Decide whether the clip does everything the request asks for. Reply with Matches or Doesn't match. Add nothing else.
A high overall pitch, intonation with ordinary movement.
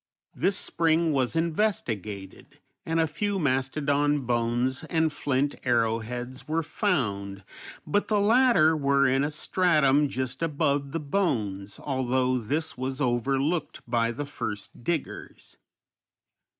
Doesn't match